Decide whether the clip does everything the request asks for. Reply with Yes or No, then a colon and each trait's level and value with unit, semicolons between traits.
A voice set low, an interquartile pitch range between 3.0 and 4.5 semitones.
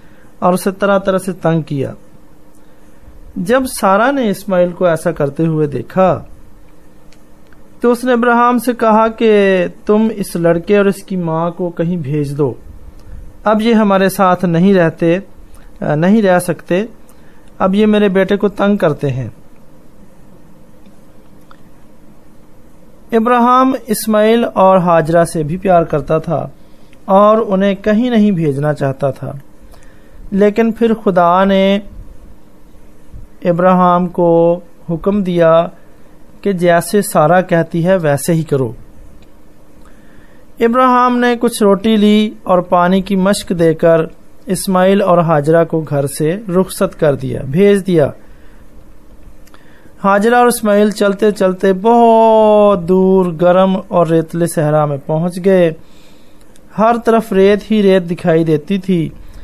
No: medium, 185 Hz; average, 4.1 semitones